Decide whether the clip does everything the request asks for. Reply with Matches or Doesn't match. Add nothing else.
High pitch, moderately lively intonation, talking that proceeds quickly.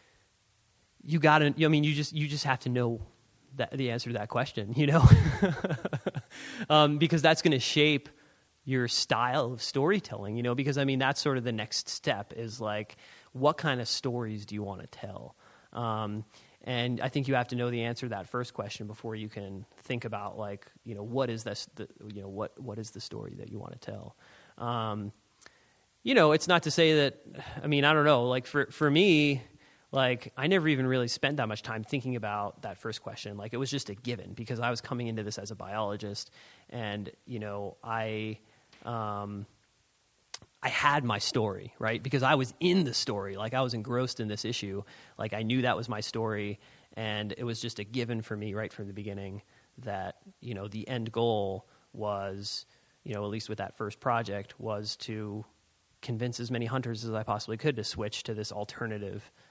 Doesn't match